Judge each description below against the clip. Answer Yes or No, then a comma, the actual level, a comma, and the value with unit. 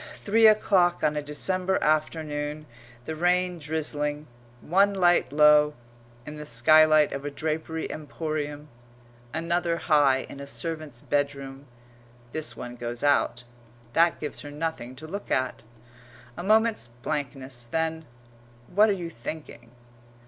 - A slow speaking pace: Yes, slow, 130 wpm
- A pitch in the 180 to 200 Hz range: No, medium, 155 Hz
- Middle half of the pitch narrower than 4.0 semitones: Yes, average, 2.7 semitones